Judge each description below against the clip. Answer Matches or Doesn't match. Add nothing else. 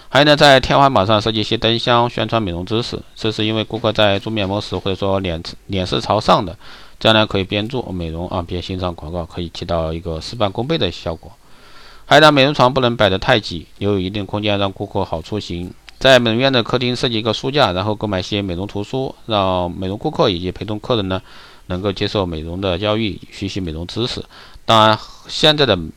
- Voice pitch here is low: Matches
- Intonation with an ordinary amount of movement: Matches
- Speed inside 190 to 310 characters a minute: Doesn't match